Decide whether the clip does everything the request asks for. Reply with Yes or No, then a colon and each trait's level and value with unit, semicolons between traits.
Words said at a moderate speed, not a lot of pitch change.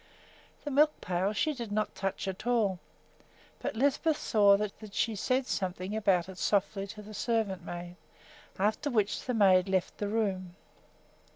No: average, 160 wpm; average, 3.1 semitones